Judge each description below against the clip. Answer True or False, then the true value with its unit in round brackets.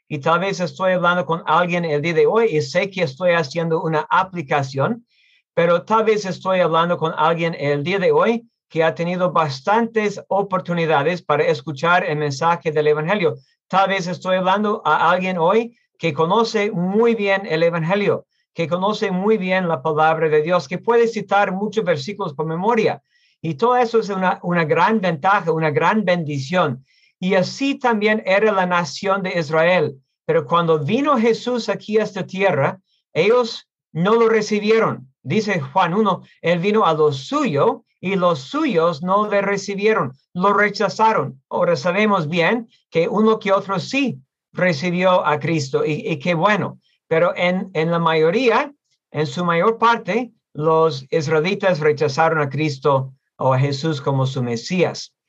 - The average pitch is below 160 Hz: False (180 Hz)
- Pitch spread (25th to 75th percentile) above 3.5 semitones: True (4.5 semitones)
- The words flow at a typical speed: True (165 wpm)